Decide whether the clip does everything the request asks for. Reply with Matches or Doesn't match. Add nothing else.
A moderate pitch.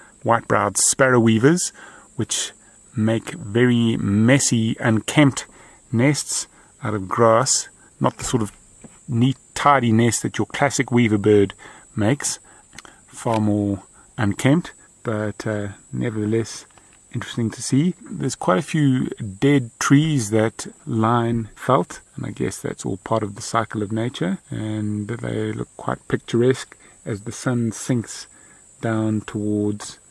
Doesn't match